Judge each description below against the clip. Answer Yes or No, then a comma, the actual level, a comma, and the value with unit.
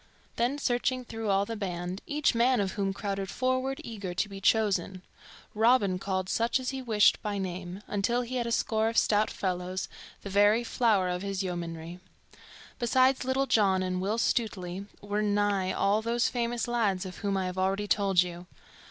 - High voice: Yes, high, 205 Hz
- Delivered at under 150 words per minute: No, average, 180 wpm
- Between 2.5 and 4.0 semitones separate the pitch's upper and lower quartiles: Yes, average, 3.7 semitones